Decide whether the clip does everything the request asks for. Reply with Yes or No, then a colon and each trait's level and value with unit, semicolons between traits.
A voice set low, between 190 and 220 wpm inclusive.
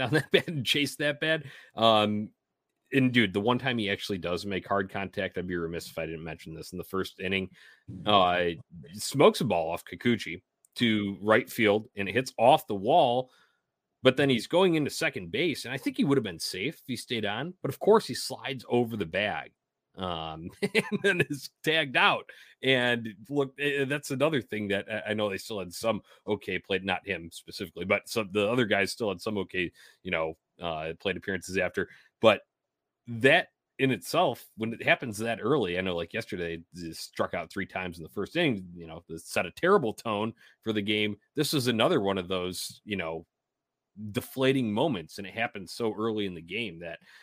Yes: low, 110 Hz; fast, 205 wpm